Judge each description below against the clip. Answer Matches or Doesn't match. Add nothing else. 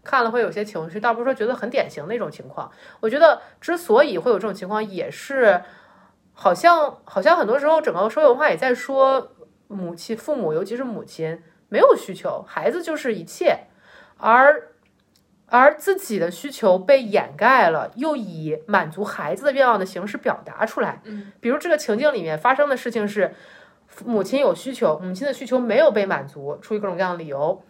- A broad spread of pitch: Matches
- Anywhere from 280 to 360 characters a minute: Matches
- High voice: Matches